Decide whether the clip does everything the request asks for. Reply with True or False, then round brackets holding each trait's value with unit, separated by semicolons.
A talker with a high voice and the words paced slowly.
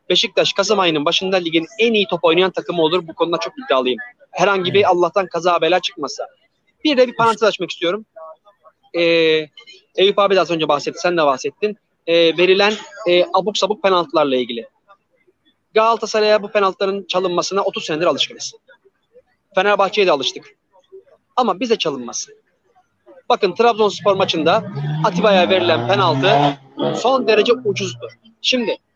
False (195 Hz; 135 wpm)